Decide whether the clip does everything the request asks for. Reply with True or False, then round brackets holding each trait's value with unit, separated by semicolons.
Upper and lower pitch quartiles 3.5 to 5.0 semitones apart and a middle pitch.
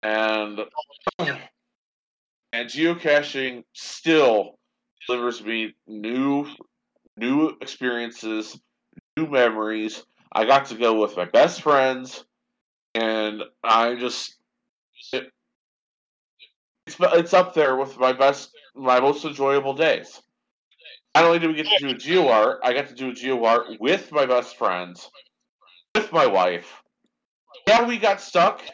False (4.0 semitones; 125 Hz)